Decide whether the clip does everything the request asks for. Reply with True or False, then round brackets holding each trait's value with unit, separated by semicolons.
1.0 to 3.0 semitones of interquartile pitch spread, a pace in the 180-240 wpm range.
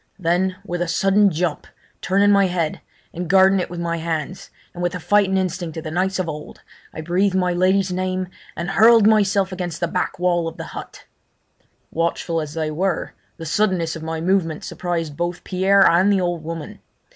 True (2.4 semitones; 190 wpm)